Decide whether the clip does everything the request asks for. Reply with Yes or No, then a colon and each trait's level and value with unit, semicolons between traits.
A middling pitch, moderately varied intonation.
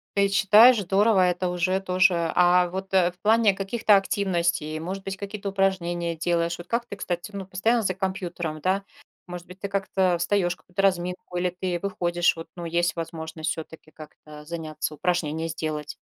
No: medium, 180 Hz; narrow, 2.3 semitones